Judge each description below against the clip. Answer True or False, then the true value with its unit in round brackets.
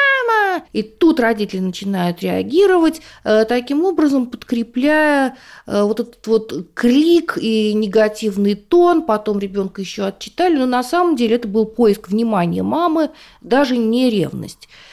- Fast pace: False (125 wpm)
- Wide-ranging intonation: True (6.4 semitones)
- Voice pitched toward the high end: True (240 Hz)